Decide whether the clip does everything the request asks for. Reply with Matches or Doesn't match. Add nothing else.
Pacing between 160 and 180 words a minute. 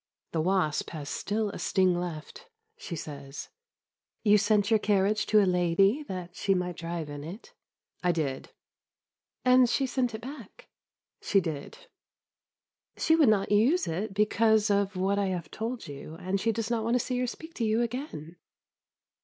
Matches